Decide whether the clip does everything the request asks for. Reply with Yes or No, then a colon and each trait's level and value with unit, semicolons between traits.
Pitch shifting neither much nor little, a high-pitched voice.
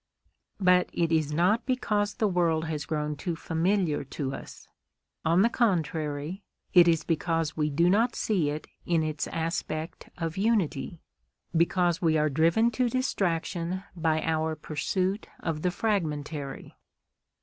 No: average, 3.3 semitones; medium, 165 Hz